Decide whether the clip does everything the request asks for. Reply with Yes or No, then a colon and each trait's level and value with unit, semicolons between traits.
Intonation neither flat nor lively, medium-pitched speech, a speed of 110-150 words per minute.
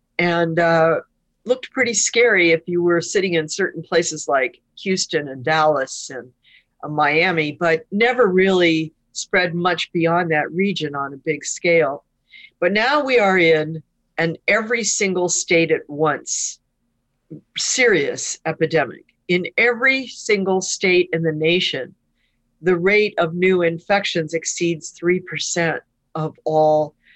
Yes: average, 3.2 semitones; medium, 170 Hz; slow, 135 wpm